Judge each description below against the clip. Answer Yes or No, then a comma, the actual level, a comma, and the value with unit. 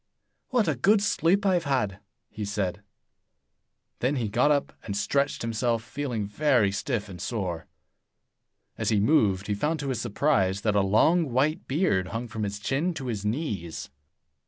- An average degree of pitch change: No, wide, 6.3 semitones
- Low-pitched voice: Yes, low, 115 Hz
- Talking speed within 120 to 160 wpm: No, average, 170 wpm